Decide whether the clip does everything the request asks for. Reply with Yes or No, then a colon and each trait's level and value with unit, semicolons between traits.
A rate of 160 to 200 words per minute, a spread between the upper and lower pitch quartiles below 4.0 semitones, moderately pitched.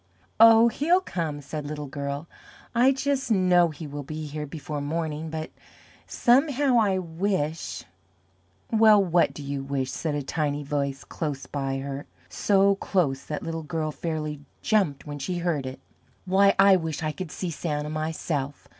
No: average, 165 wpm; average, 4.7 semitones; medium, 155 Hz